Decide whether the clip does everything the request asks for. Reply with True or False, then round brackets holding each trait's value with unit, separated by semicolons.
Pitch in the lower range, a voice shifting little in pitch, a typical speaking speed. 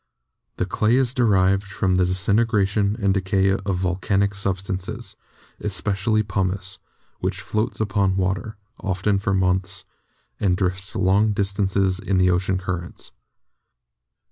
False (95 Hz; 1.6 semitones; 125 wpm)